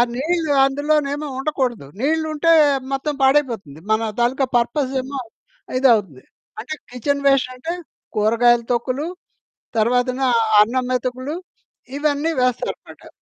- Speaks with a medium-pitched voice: No, very high, 260 Hz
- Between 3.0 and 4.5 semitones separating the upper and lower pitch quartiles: Yes, average, 3.3 semitones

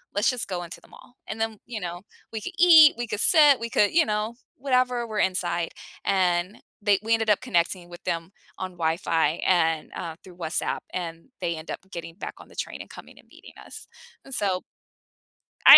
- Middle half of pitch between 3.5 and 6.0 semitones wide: Yes, average, 4.7 semitones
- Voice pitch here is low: No, high, 190 Hz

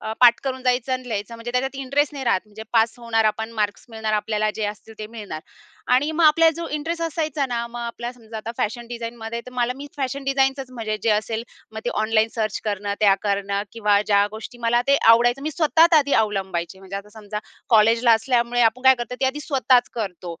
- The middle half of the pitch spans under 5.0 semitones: Yes, average, 3.3 semitones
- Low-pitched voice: No, high, 235 Hz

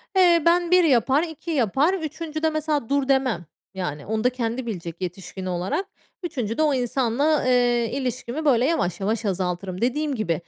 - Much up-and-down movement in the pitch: Yes, wide, 6.8 semitones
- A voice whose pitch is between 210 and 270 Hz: Yes, very high, 255 Hz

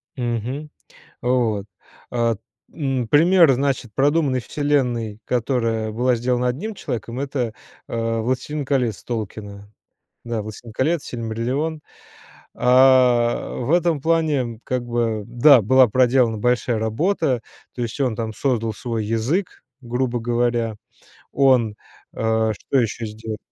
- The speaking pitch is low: Yes, low, 120 Hz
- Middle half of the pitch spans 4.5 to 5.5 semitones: No, average, 2.9 semitones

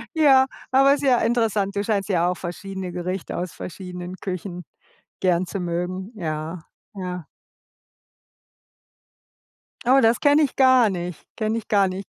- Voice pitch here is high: Yes, high, 195 Hz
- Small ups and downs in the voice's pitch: No, average, 4.3 semitones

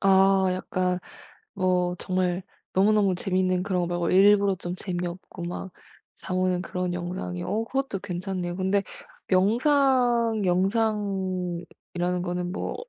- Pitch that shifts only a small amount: Yes, narrow, 2.0 semitones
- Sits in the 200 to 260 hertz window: No, medium, 185 Hz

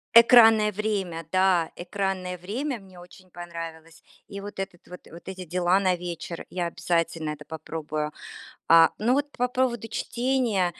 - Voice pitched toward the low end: No, medium, 185 Hz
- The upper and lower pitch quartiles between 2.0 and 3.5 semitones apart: No, average, 4.0 semitones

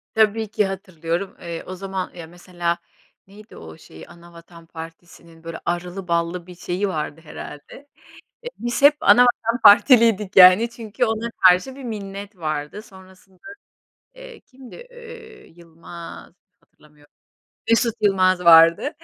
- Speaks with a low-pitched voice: No, medium, 185 Hz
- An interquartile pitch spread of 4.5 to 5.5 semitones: Yes, average, 4.8 semitones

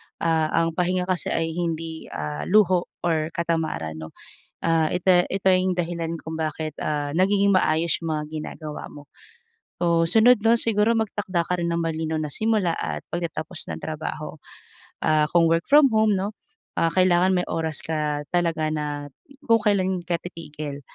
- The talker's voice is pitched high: No, medium, 165 Hz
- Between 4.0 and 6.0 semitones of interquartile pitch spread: No, average, 2.9 semitones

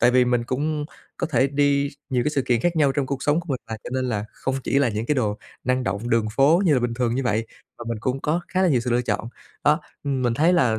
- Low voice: Yes, low, 130 Hz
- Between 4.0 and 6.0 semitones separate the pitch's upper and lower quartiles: No, average, 3.3 semitones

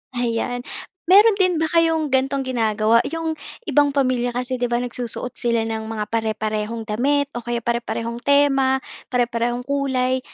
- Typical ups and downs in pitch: Yes, average, 3.2 semitones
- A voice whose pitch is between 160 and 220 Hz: No, high, 245 Hz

